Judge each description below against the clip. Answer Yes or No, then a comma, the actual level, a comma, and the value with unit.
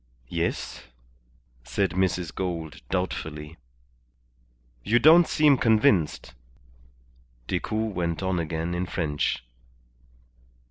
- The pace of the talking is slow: Yes, slow, 85 wpm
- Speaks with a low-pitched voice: Yes, very low, 90 Hz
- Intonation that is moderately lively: Yes, average, 4.1 semitones